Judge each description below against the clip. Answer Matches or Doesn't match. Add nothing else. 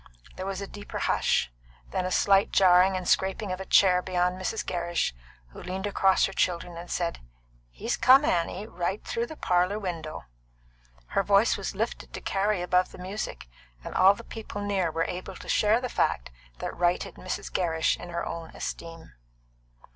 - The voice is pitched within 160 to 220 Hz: Matches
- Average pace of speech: Matches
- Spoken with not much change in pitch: Matches